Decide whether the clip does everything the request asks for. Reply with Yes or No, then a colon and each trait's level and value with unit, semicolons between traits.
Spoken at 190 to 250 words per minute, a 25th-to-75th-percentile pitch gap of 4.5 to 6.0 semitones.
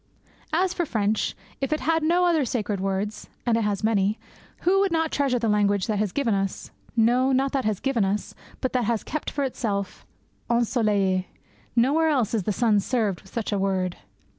Yes: average, 200 wpm; average, 5.1 semitones